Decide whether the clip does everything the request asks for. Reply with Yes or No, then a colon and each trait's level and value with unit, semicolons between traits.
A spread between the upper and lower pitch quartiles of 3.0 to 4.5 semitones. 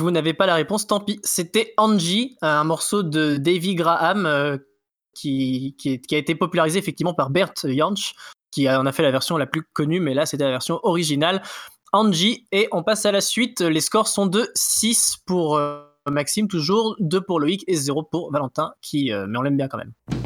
No: average, 5.3 semitones